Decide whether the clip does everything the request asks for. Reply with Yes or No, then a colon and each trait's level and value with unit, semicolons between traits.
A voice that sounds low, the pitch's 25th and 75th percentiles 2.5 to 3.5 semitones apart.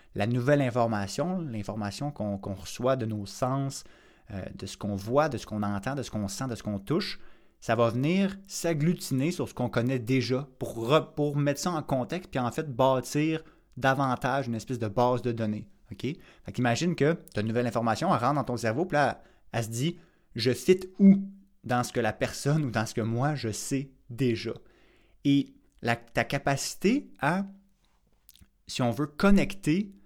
No: low, 130 Hz; average, 4.8 semitones